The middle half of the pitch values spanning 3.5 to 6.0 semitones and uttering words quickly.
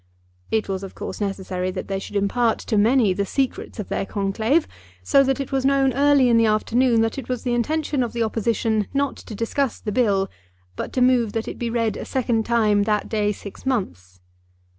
Yes: average, 3.9 semitones; fast, 210 wpm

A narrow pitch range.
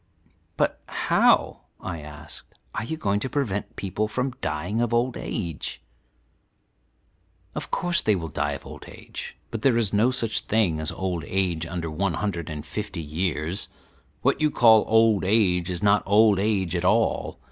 No: average, 4.8 semitones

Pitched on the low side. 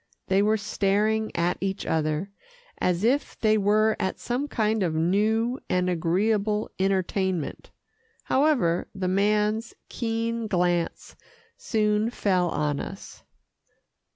No: high, 205 Hz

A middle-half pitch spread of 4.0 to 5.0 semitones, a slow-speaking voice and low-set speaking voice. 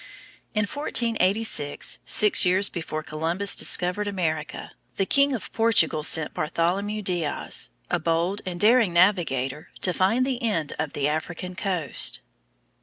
No: average, 4.6 semitones; slow, 130 wpm; medium, 180 Hz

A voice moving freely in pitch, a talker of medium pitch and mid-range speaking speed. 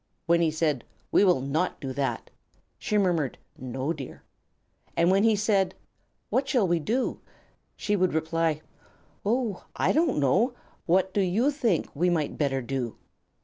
Yes: wide, 5.7 semitones; medium, 175 Hz; average, 155 wpm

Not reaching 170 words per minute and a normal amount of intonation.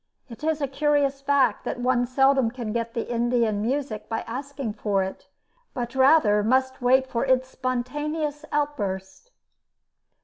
Yes: average, 145 wpm; average, 3.3 semitones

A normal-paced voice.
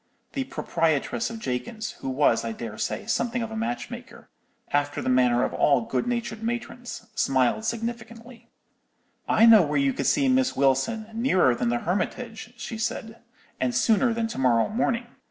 Yes: average, 170 wpm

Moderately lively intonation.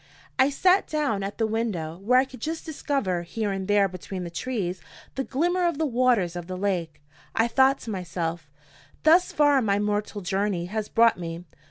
No: wide, 6.5 semitones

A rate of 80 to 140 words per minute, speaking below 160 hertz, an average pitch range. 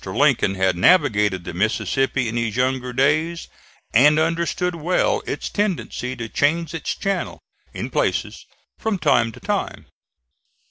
No: slow, 135 wpm; low, 135 Hz; wide, 6.6 semitones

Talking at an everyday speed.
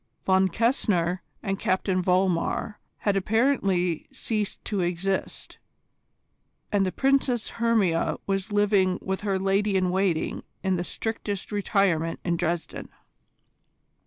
No: slow, 115 wpm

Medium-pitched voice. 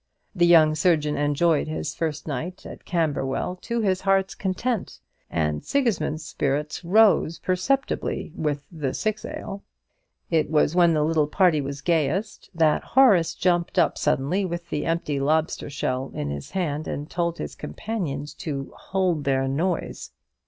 Yes: medium, 160 Hz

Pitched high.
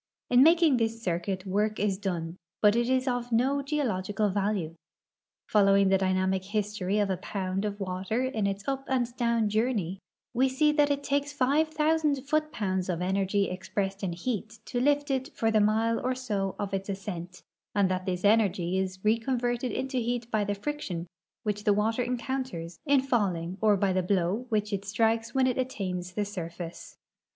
Yes: high, 210 Hz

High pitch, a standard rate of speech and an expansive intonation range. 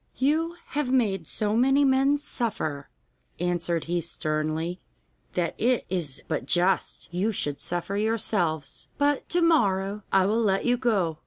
Yes: high, 195 Hz; average, 145 wpm; wide, 6.6 semitones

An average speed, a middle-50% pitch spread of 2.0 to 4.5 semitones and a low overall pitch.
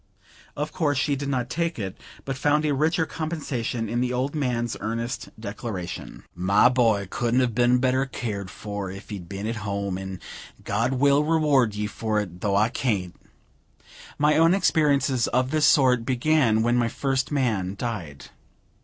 No: average, 170 wpm; average, 5.0 semitones; low, 120 Hz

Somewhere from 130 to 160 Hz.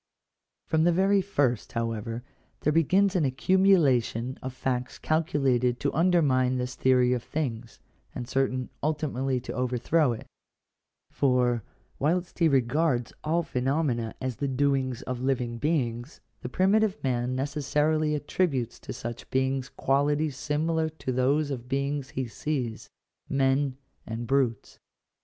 Yes: low, 135 Hz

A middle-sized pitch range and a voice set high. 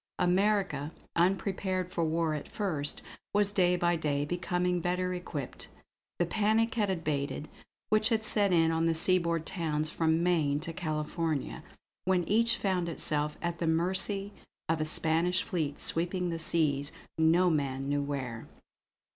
No: average, 3.1 semitones; medium, 170 Hz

